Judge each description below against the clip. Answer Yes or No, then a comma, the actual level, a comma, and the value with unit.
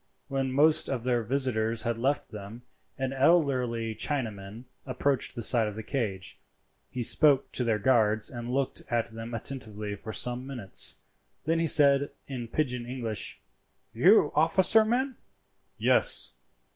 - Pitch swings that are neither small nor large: Yes, average, 3.6 semitones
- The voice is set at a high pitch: No, low, 125 Hz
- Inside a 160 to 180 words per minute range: No, average, 145 wpm